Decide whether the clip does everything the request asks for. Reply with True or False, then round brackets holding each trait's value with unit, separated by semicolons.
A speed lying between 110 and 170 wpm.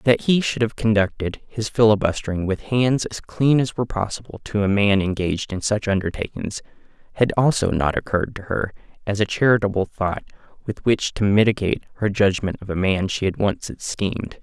False (185 wpm)